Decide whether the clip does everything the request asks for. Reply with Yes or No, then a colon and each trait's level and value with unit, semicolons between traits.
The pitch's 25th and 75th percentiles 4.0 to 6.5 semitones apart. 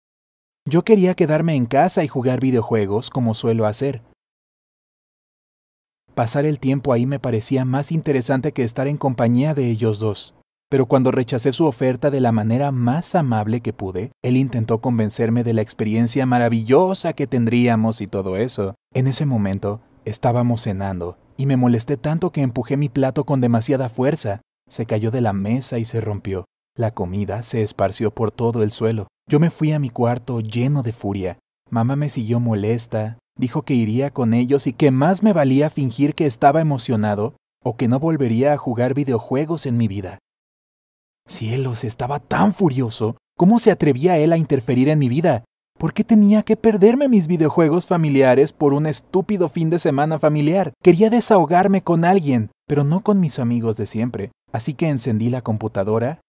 Yes: average, 4.7 semitones